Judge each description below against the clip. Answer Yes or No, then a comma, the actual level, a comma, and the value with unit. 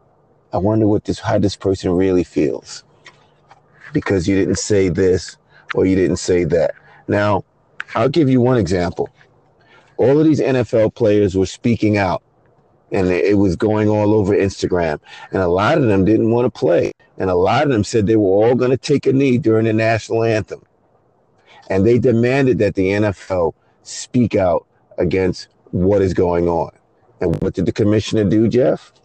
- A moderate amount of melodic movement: Yes, average, 3.4 semitones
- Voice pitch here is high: No, low, 105 Hz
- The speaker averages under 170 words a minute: No, average, 180 wpm